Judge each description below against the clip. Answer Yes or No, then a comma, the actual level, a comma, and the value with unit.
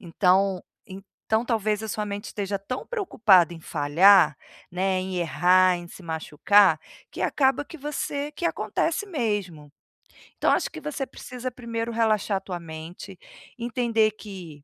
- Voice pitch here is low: No, high, 200 Hz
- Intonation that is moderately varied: Yes, average, 4.7 semitones